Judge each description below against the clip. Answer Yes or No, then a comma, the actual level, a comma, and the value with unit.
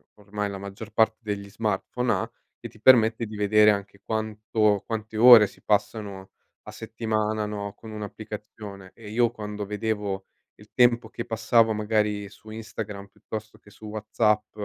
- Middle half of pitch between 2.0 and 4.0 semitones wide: No, narrow, 1.2 semitones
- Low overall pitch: Yes, low, 105 Hz